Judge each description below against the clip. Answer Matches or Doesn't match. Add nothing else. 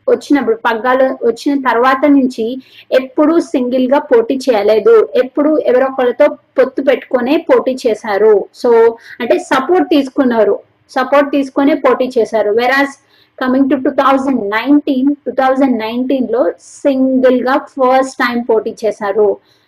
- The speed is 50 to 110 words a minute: Doesn't match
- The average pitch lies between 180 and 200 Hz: Doesn't match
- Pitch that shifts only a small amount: Doesn't match